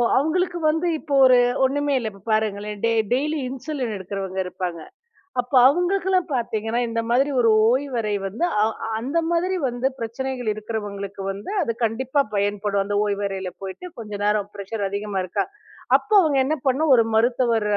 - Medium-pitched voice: No, high, 230 Hz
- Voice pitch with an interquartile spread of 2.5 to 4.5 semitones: No, average, 5.1 semitones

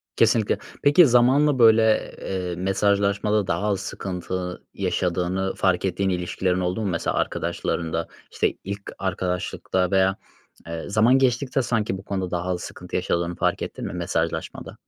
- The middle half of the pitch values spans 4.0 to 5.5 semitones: No, average, 3.3 semitones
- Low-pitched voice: Yes, very low, 95 Hz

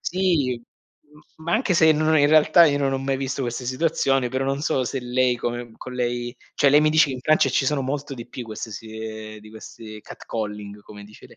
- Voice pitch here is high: No, low, 130 Hz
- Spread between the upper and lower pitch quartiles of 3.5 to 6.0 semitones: Yes, average, 3.9 semitones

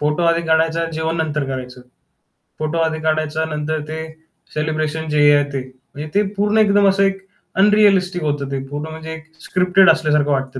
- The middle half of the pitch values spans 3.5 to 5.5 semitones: No, average, 3.1 semitones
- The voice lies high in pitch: No, medium, 160 Hz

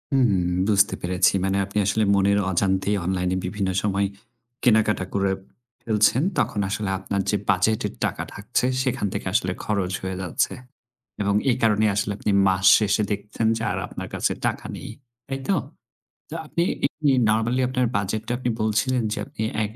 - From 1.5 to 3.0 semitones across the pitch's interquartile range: Yes, narrow, 2.6 semitones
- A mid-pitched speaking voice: No, low, 105 Hz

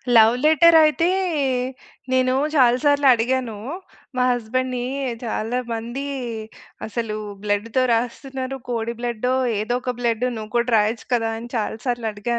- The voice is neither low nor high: No, high, 240 Hz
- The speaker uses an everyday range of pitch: No, narrow, 2.3 semitones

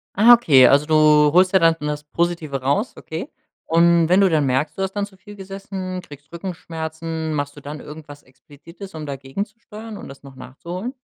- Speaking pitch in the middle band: Yes, medium, 160 Hz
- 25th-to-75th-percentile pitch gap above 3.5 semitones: Yes, average, 4.4 semitones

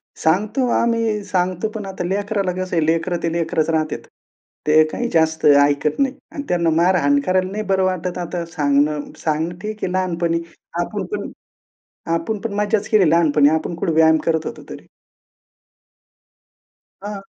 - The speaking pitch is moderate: Yes, medium, 175 Hz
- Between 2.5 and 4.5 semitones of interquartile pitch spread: Yes, average, 4.0 semitones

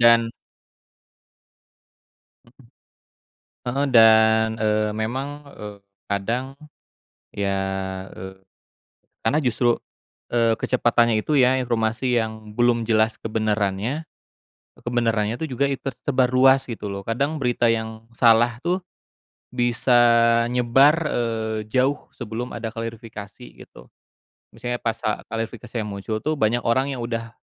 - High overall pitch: No, low, 115 Hz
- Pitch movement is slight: Yes, narrow, 2.2 semitones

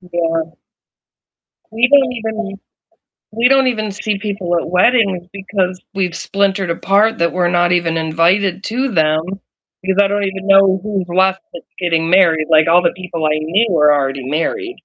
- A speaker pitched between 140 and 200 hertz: Yes, medium, 185 Hz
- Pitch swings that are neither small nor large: Yes, average, 3.3 semitones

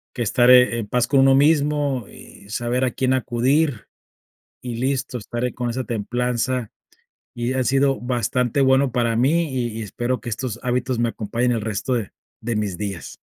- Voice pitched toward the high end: No, low, 125 Hz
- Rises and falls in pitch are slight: Yes, narrow, 2.0 semitones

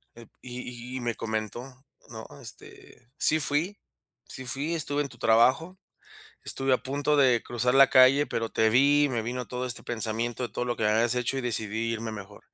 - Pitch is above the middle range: No, low, 125 Hz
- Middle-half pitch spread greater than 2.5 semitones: Yes, average, 2.9 semitones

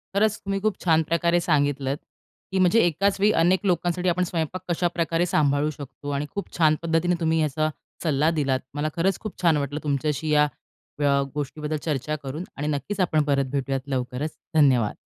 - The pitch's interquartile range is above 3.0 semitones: Yes, average, 3.4 semitones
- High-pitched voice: No, medium, 155 Hz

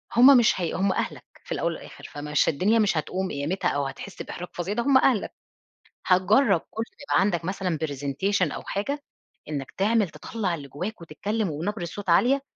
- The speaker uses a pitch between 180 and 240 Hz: Yes, high, 190 Hz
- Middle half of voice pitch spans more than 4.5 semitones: Yes, average, 5.1 semitones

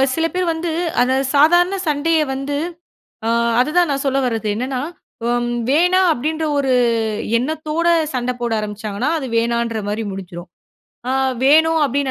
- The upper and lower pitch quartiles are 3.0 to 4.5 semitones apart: No, average, 5.2 semitones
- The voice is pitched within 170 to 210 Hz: No, very high, 275 Hz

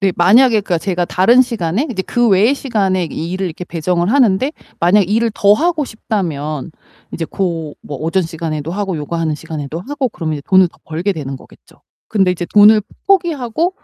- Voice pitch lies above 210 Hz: No, high, 190 Hz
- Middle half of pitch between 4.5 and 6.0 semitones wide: Yes, average, 5.1 semitones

